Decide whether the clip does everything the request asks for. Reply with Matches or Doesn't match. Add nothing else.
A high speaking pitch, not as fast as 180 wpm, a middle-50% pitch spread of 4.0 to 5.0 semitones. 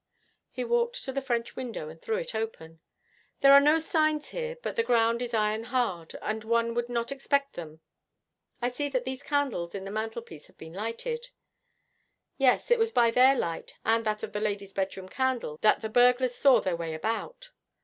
Doesn't match